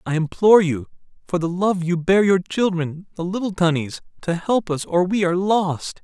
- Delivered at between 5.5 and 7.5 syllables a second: No, 5.1 syllables/s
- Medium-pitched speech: Yes, medium, 180 Hz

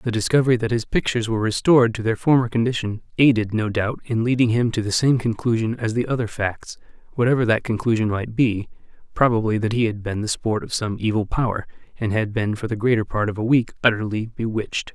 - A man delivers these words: Yes, male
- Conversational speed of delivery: No, fast, 210 wpm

